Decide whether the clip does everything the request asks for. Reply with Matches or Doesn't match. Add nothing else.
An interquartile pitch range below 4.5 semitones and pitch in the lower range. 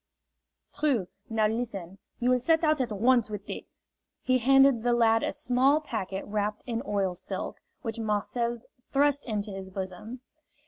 Doesn't match